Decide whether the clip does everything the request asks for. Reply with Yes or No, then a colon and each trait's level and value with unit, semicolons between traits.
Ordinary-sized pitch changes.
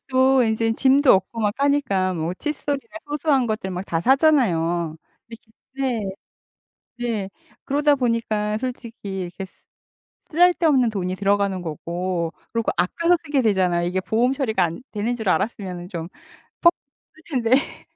No: wide, 6.3 semitones